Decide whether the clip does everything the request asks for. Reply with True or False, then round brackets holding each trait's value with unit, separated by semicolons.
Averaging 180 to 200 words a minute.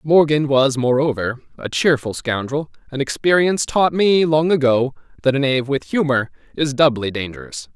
False (155 wpm)